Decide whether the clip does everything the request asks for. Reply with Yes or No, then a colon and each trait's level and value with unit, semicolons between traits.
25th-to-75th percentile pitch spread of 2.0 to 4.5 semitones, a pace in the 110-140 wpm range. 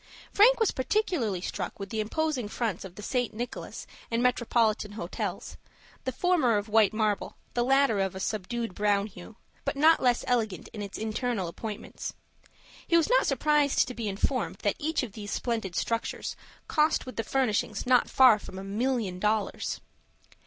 No: average, 4.1 semitones; average, 170 wpm